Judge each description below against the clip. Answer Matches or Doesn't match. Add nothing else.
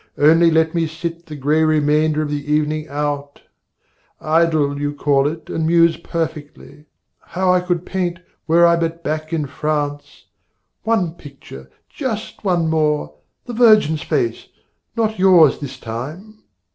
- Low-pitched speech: Doesn't match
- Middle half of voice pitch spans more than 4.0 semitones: Doesn't match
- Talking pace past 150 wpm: Doesn't match